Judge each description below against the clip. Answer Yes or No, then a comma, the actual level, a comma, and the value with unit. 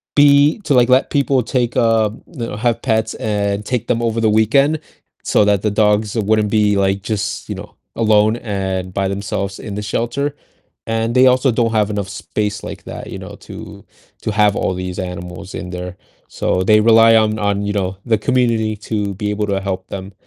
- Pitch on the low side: Yes, low, 105 Hz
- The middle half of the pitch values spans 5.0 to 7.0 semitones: No, narrow, 2.5 semitones